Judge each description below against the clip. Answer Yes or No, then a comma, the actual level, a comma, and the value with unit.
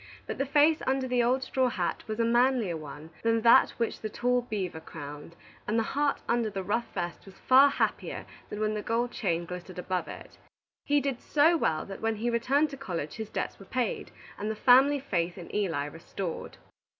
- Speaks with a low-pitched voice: No, high, 225 Hz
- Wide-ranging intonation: Yes, wide, 6.0 semitones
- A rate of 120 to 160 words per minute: No, fast, 205 wpm